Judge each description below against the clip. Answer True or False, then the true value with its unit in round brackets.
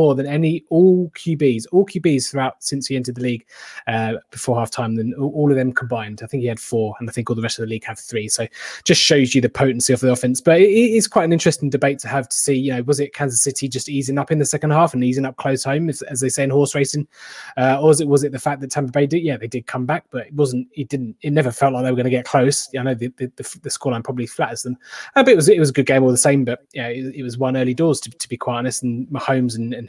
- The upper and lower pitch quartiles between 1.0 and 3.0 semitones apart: True (2.7 semitones)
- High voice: False (135 Hz)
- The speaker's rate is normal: False (305 wpm)